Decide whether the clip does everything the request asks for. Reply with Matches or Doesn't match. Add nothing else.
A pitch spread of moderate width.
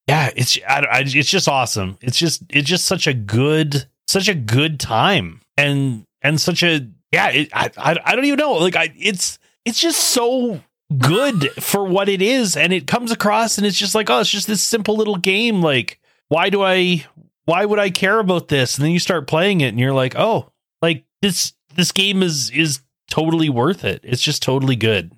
Doesn't match